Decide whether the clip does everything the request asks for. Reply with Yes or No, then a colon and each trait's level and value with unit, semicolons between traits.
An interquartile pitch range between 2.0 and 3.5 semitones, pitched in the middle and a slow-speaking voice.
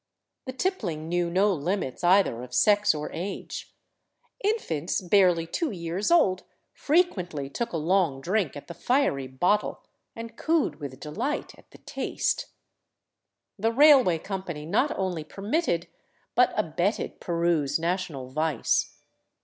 No: average, 5.1 semitones; medium, 180 Hz; slow, 130 wpm